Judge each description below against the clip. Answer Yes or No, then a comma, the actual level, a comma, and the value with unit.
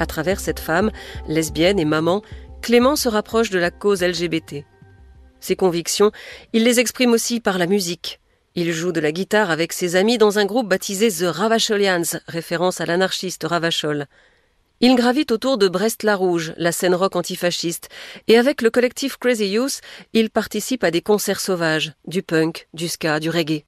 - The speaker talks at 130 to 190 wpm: Yes, average, 175 wpm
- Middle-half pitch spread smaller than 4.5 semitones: No, average, 4.8 semitones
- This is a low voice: No, medium, 185 Hz